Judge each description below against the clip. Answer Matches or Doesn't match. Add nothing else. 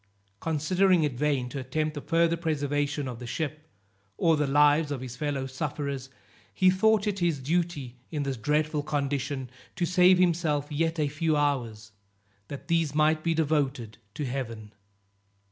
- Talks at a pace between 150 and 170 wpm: Matches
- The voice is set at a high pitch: Doesn't match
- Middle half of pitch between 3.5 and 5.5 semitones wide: Doesn't match